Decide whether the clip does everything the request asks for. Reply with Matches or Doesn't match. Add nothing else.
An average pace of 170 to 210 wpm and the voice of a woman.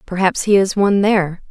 Matches